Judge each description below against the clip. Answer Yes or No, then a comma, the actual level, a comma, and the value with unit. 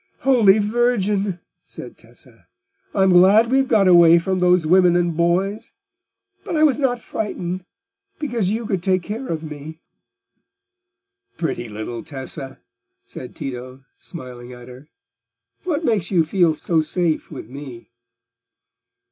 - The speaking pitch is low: No, medium, 180 Hz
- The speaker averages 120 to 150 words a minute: Yes, average, 140 wpm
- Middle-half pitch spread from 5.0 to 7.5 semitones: Yes, wide, 5.5 semitones